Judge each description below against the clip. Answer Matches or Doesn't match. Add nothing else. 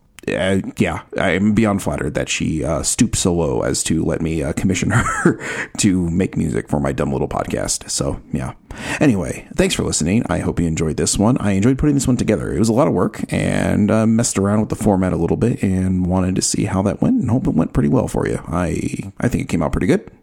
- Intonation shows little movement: Doesn't match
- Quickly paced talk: Matches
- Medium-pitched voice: Doesn't match